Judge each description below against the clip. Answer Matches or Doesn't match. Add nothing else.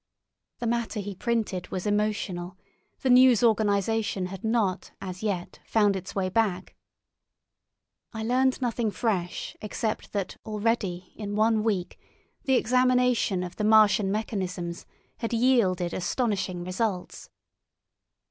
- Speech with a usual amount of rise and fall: Matches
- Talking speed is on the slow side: Matches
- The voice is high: Matches